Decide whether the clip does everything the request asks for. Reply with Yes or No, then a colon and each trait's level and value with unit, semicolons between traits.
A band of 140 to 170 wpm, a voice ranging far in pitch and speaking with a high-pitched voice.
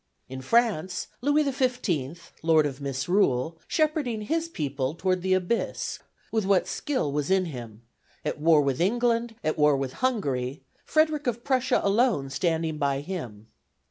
No: average, 145 wpm; wide, 9.0 semitones; medium, 175 Hz